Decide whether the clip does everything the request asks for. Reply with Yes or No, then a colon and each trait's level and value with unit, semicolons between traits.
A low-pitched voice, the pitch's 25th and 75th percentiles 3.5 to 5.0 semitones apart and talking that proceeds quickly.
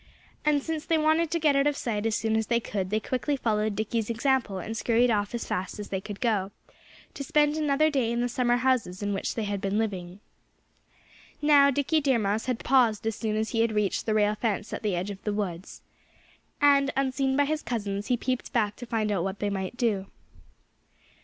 No: high, 225 Hz; average, 4.5 semitones; fast, 220 wpm